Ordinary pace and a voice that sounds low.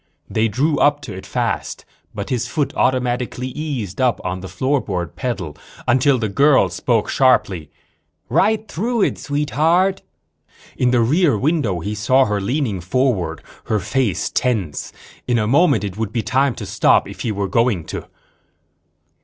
Yes: average, 160 wpm; low, 125 Hz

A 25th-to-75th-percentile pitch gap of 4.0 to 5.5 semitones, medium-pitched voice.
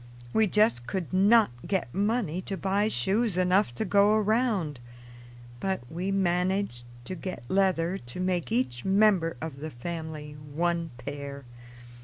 Yes: average, 5.0 semitones; medium, 180 Hz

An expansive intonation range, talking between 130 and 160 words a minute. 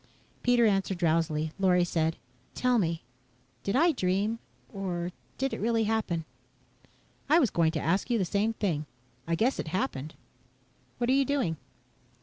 Yes: wide, 5.9 semitones; average, 155 wpm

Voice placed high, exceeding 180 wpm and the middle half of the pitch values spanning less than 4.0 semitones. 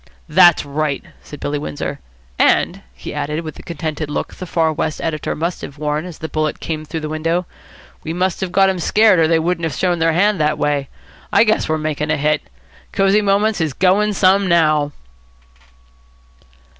No: medium, 160 Hz; average, 190 wpm; average, 3.1 semitones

